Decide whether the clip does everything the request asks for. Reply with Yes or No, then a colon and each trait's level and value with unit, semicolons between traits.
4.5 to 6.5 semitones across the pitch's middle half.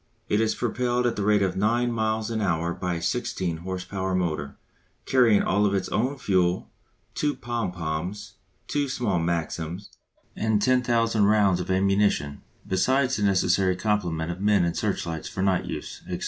No: average, 4.1 semitones